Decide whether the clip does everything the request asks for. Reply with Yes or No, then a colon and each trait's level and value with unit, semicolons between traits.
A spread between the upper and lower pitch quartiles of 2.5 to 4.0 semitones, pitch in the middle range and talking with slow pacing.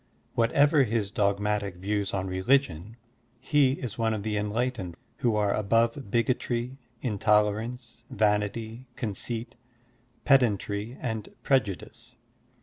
No: average, 3.0 semitones; low, 110 Hz; slow, 115 wpm